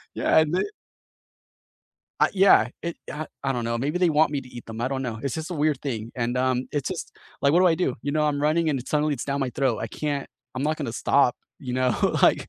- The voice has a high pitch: No, medium, 140 Hz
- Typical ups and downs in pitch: Yes, average, 3.5 semitones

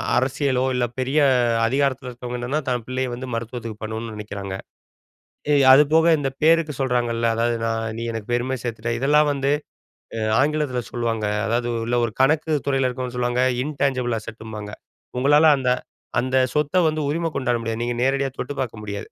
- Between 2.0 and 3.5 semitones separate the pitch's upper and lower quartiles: Yes, average, 3.0 semitones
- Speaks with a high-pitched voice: No, low, 125 Hz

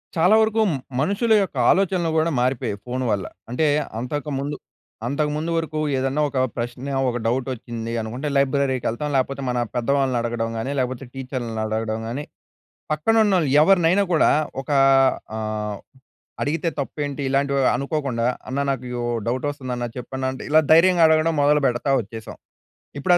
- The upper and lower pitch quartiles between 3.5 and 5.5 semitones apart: Yes, average, 4.1 semitones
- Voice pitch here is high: No, low, 135 Hz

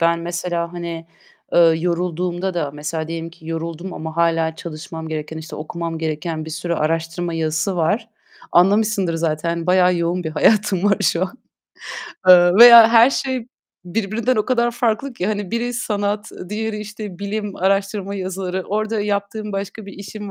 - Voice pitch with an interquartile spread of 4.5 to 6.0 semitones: No, average, 4.0 semitones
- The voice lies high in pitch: No, medium, 180 Hz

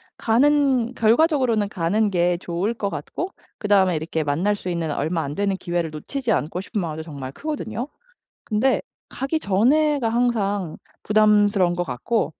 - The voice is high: Yes, high, 205 Hz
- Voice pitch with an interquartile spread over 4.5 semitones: Yes, wide, 5.6 semitones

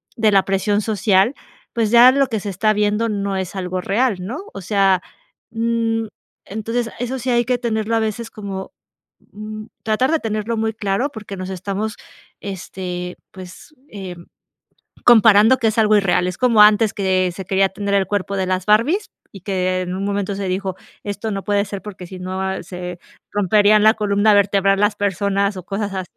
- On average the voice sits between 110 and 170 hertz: No, high, 205 Hz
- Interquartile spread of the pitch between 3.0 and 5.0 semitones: No, narrow, 2.5 semitones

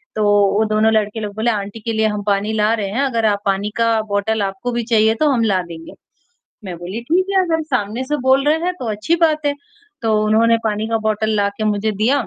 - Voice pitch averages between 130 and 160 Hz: No, high, 220 Hz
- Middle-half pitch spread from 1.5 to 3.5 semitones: Yes, narrow, 2.4 semitones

